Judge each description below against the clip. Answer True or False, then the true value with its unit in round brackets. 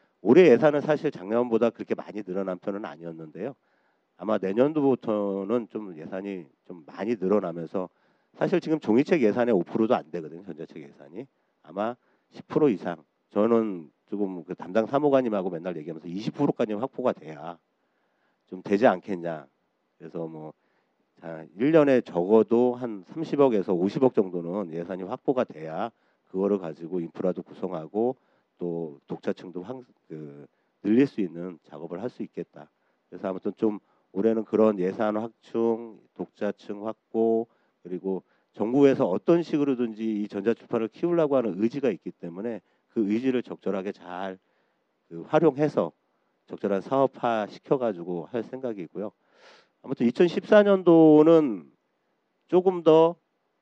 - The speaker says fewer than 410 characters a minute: True (290 characters per minute)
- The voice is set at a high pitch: False (110 Hz)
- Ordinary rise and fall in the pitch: False (6.0 semitones)